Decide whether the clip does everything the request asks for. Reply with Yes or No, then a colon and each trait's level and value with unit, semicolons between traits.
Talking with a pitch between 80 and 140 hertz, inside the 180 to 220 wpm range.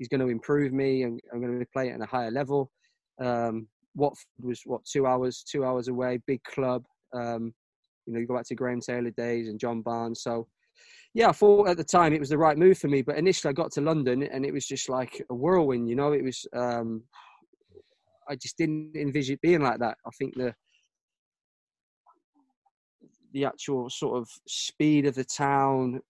Yes: low, 135 Hz; fast, 205 wpm